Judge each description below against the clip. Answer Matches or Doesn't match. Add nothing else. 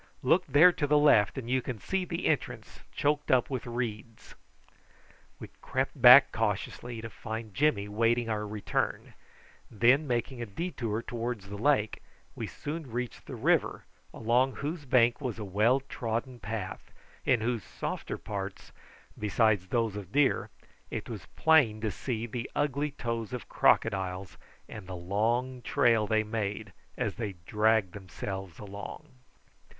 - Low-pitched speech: Matches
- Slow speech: Doesn't match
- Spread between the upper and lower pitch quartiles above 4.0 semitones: Doesn't match